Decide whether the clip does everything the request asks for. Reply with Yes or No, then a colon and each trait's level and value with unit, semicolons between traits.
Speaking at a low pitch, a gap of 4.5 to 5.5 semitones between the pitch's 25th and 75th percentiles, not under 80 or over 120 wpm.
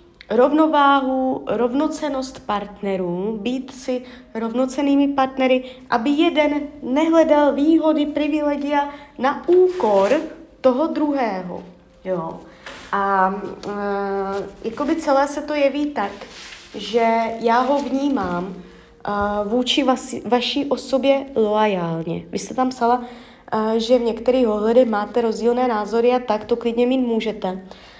No: very high, 250 Hz; average, 4.8 semitones; slow, 115 wpm